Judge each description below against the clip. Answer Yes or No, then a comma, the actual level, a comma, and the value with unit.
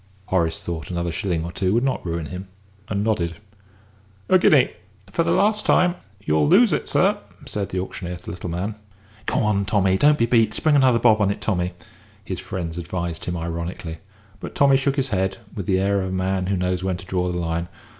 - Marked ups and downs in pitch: No, average, 3.8 semitones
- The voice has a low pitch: Yes, very low, 95 Hz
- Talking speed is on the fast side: Yes, fast, 215 wpm